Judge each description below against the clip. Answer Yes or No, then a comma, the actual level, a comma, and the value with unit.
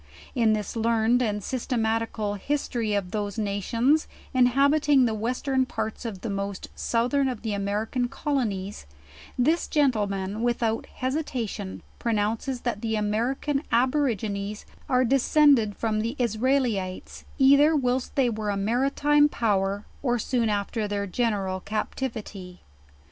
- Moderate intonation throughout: Yes, average, 3.9 semitones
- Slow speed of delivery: Yes, slow, 125 wpm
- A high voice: Yes, high, 230 Hz